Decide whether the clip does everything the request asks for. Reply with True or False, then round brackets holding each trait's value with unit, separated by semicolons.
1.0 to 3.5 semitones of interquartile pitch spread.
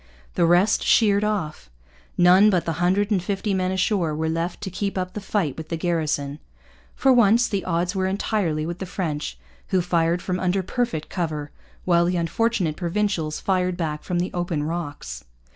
True (3.2 semitones)